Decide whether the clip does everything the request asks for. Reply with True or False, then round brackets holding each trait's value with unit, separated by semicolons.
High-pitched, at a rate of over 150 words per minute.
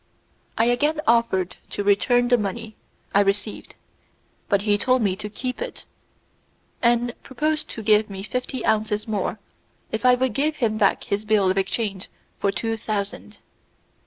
True (220 Hz; 160 wpm)